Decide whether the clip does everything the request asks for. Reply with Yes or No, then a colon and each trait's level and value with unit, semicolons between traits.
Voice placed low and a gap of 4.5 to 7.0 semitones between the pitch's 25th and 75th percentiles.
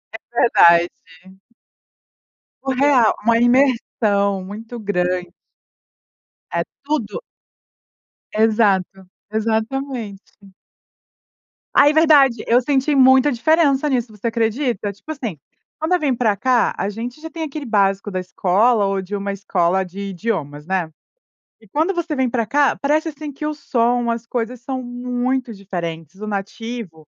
No: high, 230 Hz; average, 5.1 semitones